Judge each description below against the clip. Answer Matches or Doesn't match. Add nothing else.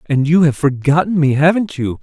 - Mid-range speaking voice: Matches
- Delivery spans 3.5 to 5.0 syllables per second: Doesn't match